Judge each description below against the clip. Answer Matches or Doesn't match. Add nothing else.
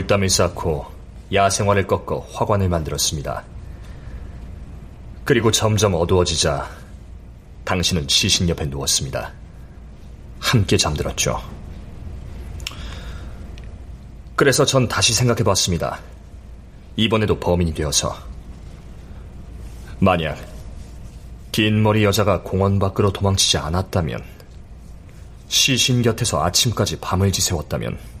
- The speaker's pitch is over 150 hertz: Doesn't match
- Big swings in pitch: Doesn't match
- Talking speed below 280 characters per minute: Matches